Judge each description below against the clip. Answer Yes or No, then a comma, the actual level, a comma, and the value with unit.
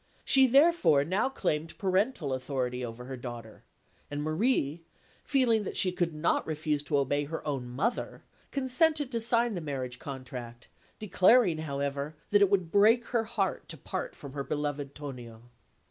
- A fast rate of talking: No, average, 160 wpm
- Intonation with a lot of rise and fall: Yes, wide, 8.0 semitones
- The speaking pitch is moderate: Yes, medium, 155 Hz